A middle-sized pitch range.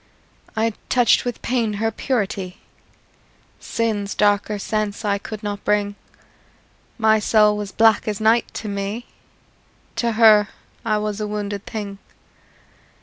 No: narrow, 1.5 semitones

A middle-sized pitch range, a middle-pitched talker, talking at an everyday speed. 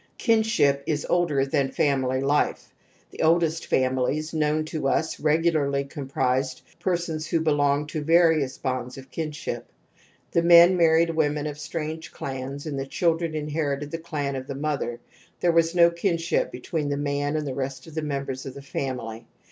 Yes: average, 3.0 semitones; medium, 150 Hz; average, 170 wpm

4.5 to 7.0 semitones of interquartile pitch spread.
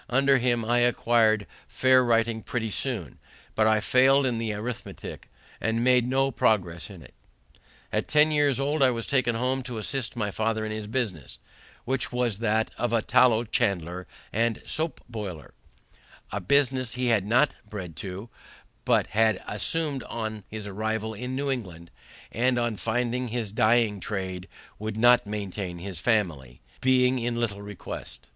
No: average, 3.4 semitones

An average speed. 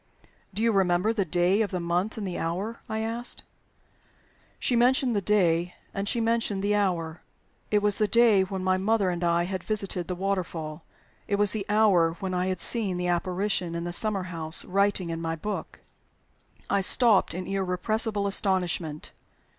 Yes: average, 180 wpm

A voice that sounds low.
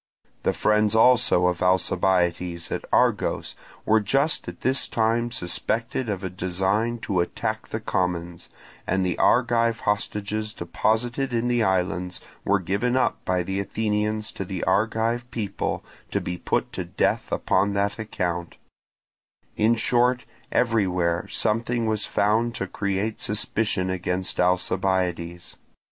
Yes: low, 100 Hz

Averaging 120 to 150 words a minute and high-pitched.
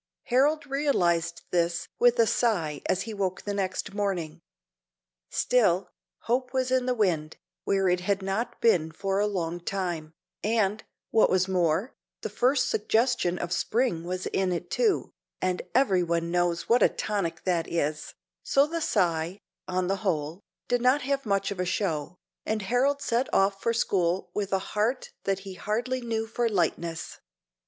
No: average, 165 wpm; high, 195 Hz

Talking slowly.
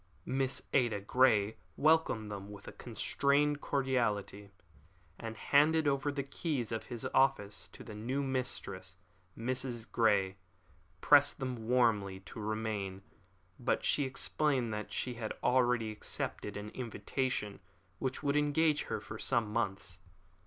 Yes: slow, 130 wpm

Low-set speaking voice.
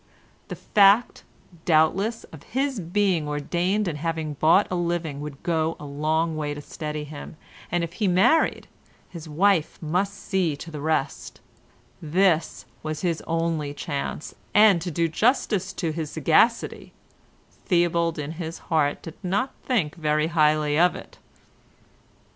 No: medium, 165 Hz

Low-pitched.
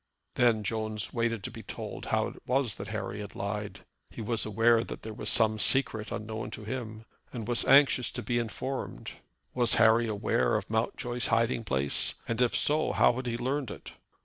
Yes: low, 115 Hz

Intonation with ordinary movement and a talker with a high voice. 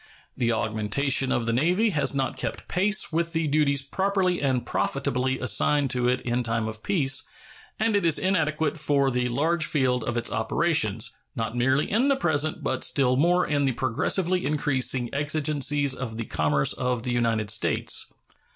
No: average, 4.4 semitones; low, 135 Hz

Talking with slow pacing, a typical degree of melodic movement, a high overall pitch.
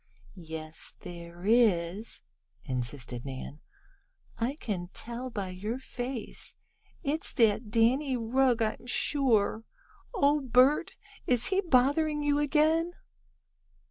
No: slow, 105 wpm; wide, 7.2 semitones; high, 235 Hz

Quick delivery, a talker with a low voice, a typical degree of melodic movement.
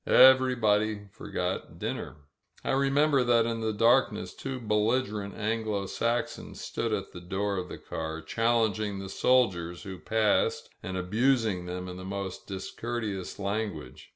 No: average, 140 wpm; low, 105 Hz; average, 3.6 semitones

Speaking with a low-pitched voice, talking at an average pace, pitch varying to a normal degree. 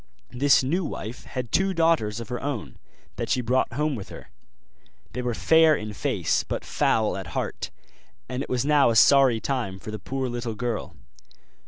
Yes: low, 125 Hz; average, 185 wpm; average, 3.9 semitones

